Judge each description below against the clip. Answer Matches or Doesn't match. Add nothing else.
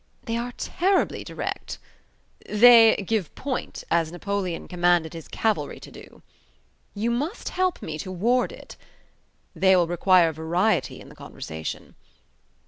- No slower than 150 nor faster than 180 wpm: Doesn't match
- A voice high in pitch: Matches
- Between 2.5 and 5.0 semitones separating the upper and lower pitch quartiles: Doesn't match